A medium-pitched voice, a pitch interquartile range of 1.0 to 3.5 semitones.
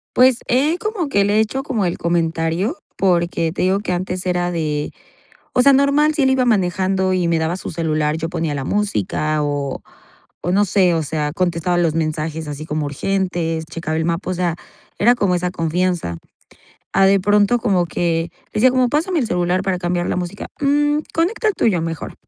No: medium, 180 Hz; average, 4.4 semitones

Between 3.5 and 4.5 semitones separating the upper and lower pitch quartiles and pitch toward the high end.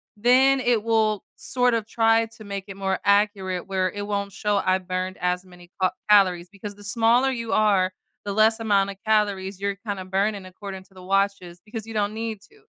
No: narrow, 2.6 semitones; high, 200 Hz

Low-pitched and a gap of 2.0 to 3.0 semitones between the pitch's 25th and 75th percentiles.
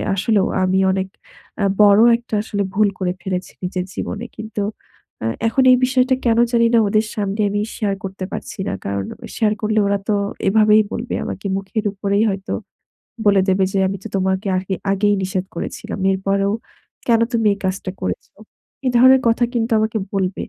No: high, 205 Hz; narrow, 2.5 semitones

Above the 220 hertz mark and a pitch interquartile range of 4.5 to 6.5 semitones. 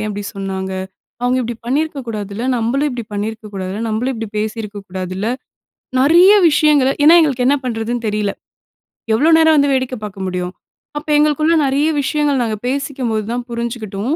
Yes: high, 235 Hz; average, 5.0 semitones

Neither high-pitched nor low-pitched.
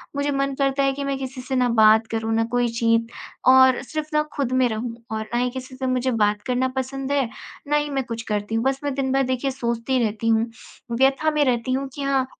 No: very high, 260 Hz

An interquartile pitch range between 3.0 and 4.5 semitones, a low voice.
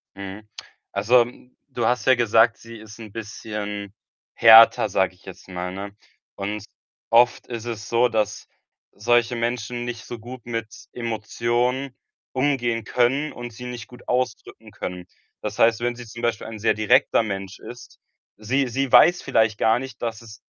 No: narrow, 2.4 semitones; low, 115 Hz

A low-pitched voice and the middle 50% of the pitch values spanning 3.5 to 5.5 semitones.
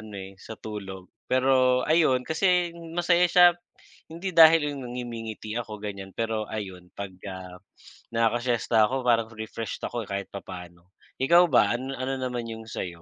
Yes: low, 115 Hz; average, 4.6 semitones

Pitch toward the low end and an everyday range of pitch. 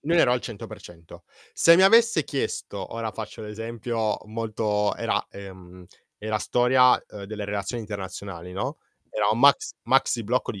Yes: low, 110 Hz; average, 3.4 semitones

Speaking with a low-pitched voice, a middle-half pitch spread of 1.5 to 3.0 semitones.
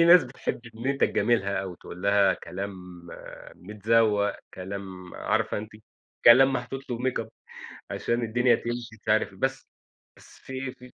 No: low, 115 Hz; average, 4.1 semitones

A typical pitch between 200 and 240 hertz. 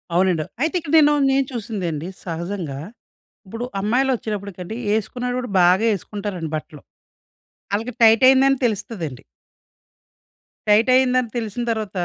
Yes: high, 215 Hz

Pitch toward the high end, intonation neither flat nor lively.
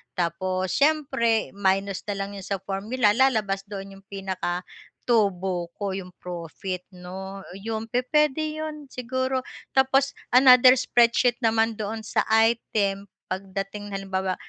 Yes: high, 205 Hz; average, 4.4 semitones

